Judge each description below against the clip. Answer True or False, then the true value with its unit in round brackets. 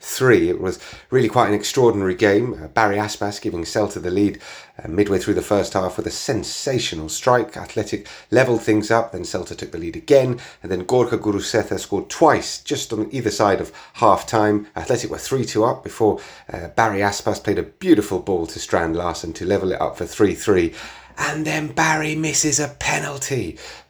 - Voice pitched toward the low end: True (105 Hz)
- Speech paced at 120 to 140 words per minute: False (190 wpm)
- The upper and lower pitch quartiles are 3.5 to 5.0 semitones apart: True (3.8 semitones)